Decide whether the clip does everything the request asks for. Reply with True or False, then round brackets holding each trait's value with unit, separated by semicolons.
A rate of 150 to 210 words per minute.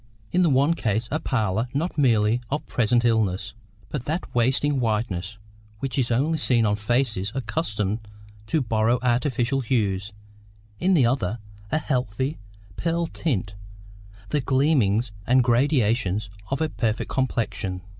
False (135 wpm)